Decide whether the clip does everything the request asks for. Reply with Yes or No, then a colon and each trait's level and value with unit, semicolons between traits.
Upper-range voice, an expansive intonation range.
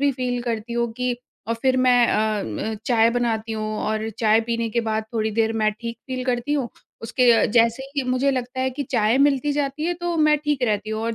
No: high, 240 Hz; average, 2.8 semitones